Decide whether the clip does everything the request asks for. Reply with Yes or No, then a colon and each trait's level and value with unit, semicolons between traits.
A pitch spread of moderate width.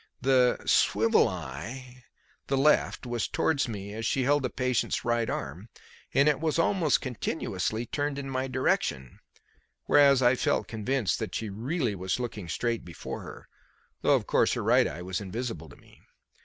Yes: average, 4.7 semitones